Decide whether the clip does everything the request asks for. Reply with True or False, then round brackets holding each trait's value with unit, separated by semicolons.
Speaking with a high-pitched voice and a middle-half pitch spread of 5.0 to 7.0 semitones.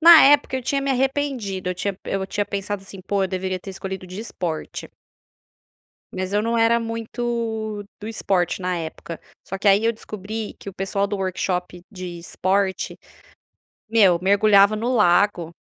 False (200 Hz; 3.4 semitones)